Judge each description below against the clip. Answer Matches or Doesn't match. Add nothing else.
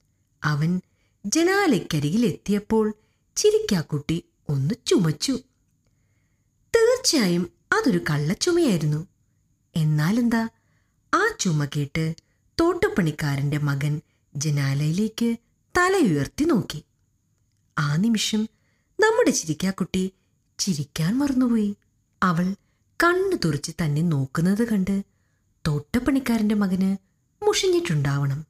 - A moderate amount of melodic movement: Doesn't match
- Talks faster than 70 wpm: Doesn't match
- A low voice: Doesn't match